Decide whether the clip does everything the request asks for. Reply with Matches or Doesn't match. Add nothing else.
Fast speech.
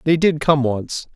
Matches